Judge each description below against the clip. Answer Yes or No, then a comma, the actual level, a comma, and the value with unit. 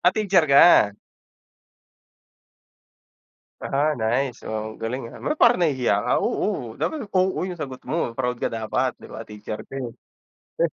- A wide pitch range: Yes, wide, 7.2 semitones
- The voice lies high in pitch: No, low, 130 Hz